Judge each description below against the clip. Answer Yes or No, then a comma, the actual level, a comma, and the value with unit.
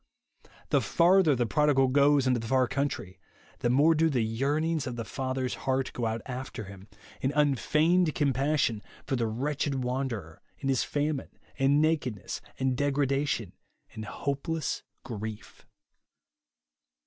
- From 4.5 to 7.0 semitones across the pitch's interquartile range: No, average, 3.4 semitones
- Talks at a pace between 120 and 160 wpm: Yes, average, 140 wpm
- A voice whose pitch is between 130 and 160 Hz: Yes, low, 135 Hz